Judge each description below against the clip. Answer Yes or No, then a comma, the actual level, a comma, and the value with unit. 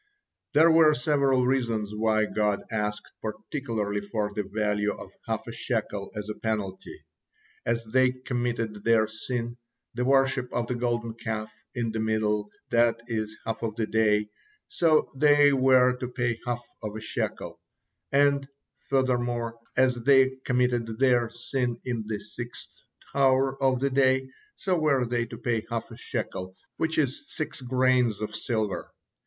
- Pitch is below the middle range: Yes, low, 120 Hz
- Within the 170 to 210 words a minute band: No, average, 155 wpm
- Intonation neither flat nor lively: Yes, average, 3.2 semitones